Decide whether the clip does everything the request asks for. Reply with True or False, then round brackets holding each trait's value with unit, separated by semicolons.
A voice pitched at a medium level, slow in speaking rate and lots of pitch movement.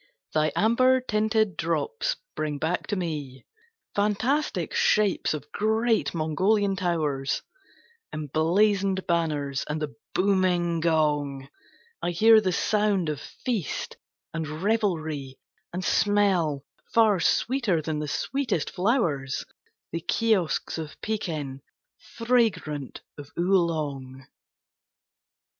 True (175 Hz; 100 wpm; 5.8 semitones)